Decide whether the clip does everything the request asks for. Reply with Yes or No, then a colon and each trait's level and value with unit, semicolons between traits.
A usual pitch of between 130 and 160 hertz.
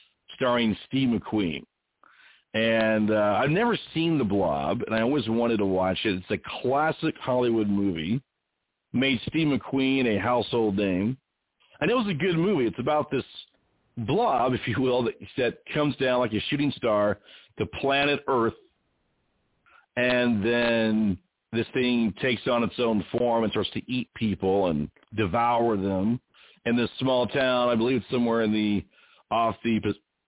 No: low, 115 Hz